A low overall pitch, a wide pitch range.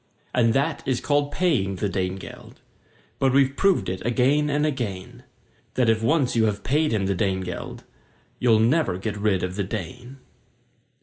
Yes: low, 115 Hz; wide, 6.2 semitones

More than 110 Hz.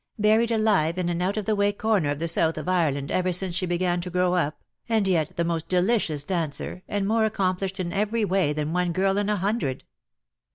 Yes: medium, 185 Hz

